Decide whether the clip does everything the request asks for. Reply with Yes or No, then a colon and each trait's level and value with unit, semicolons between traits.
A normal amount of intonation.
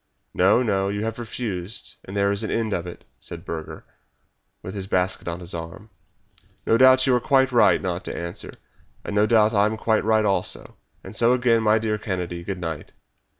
Yes: average, 3.9 semitones